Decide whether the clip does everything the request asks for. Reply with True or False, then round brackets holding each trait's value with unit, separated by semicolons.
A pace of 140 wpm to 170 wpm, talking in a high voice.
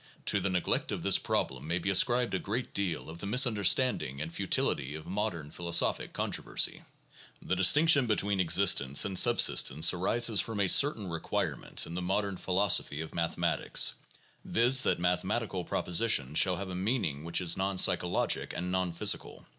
False (160 wpm; 95 Hz)